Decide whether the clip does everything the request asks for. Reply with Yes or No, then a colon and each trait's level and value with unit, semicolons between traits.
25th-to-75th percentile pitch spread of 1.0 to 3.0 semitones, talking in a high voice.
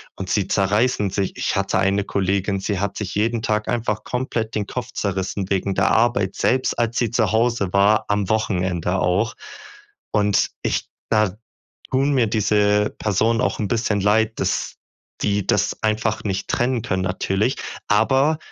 No: narrow, 2.6 semitones; low, 105 Hz